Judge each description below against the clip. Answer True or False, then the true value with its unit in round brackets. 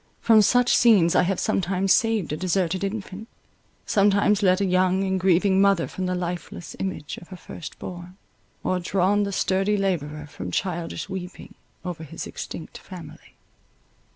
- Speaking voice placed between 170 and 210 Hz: True (185 Hz)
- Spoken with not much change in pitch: True (2.1 semitones)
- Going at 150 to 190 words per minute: True (155 wpm)